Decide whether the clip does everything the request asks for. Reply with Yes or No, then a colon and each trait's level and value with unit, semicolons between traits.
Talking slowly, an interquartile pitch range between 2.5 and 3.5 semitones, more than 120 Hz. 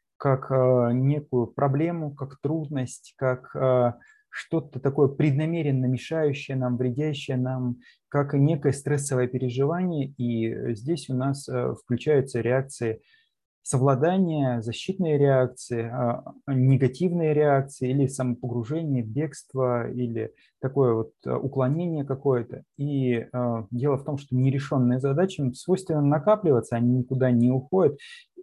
Yes: slow, 105 wpm; average, 3.0 semitones; low, 135 Hz